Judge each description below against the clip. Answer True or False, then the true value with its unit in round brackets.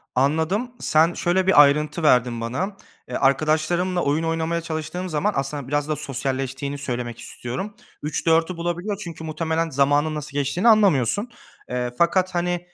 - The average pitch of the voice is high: False (155 Hz)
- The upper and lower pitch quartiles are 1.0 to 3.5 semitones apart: False (3.9 semitones)